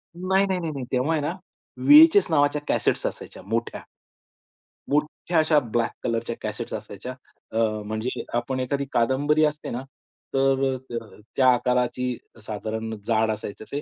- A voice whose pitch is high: No, low, 130 Hz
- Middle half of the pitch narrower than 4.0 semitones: No, average, 4.5 semitones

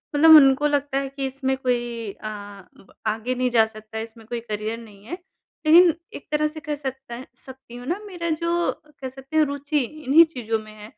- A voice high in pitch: Yes, very high, 265 Hz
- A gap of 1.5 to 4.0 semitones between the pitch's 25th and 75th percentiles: No, average, 4.5 semitones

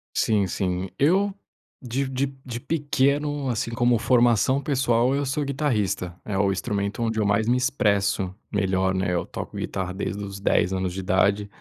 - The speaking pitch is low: Yes, low, 110 Hz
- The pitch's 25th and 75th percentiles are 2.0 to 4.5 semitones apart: No, average, 5.3 semitones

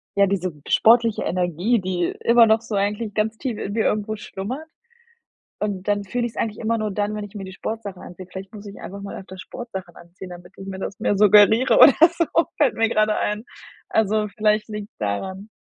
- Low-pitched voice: No, high, 210 Hz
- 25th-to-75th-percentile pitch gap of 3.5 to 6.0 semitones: No, narrow, 2.5 semitones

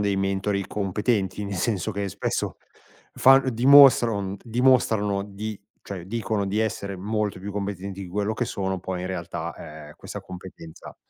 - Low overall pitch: Yes, low, 100 Hz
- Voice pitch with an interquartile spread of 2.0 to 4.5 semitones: Yes, narrow, 2.4 semitones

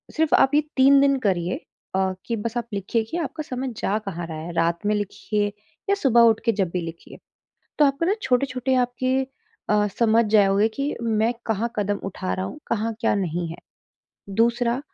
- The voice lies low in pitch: No, high, 225 Hz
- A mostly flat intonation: No, average, 5.0 semitones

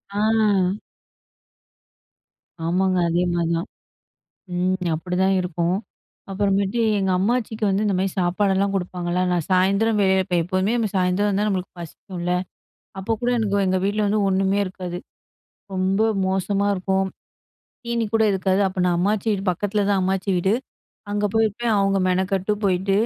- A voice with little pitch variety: Yes, narrow, 1.8 semitones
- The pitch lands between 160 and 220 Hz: Yes, high, 190 Hz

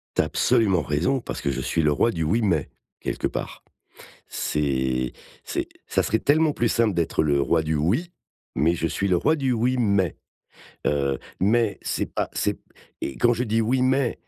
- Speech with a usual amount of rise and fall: No, wide, 7.8 semitones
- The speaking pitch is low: Yes, very low, 95 Hz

